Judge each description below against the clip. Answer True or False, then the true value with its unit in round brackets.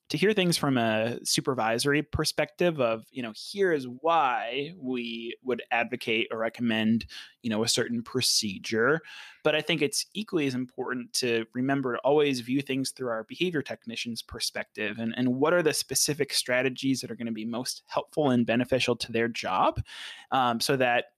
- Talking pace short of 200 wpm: True (180 wpm)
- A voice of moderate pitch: False (125 Hz)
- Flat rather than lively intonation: False (3.7 semitones)